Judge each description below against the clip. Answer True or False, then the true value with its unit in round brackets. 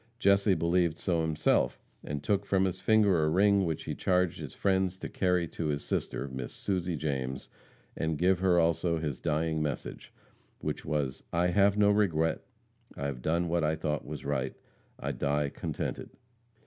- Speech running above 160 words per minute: True (170 wpm)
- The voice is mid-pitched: False (85 Hz)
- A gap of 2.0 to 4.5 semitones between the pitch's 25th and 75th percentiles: True (3.6 semitones)